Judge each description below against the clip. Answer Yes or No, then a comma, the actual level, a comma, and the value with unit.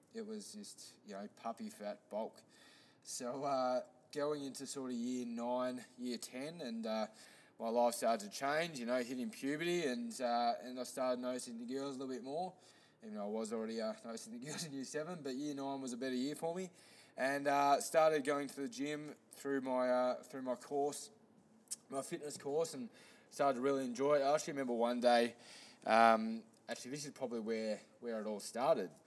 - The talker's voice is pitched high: No, low, 130 Hz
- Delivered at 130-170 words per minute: No, fast, 205 wpm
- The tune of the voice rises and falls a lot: No, average, 3.7 semitones